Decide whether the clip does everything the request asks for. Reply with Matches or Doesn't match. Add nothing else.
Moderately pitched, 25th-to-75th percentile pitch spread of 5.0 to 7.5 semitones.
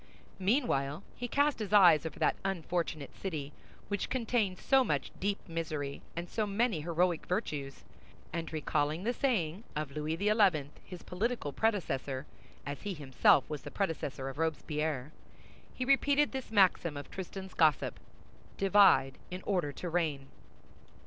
Matches